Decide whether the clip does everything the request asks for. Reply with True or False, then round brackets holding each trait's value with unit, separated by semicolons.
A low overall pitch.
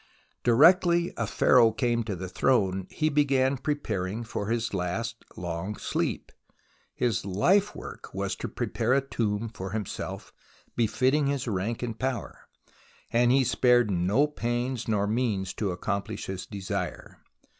True (115 Hz)